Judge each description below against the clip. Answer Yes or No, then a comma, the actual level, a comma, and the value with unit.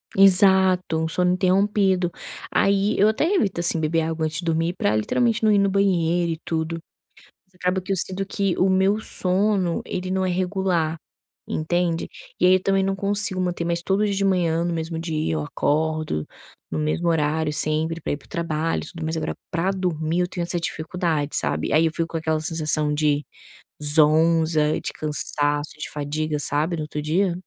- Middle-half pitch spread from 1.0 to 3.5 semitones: Yes, average, 3.1 semitones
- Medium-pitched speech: Yes, medium, 170 Hz